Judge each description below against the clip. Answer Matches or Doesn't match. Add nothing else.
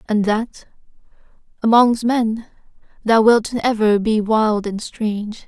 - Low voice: Doesn't match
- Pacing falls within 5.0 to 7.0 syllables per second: Doesn't match